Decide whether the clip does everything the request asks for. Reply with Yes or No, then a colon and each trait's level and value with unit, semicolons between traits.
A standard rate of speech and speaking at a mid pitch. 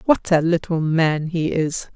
Yes: average, 185 wpm; medium, 165 Hz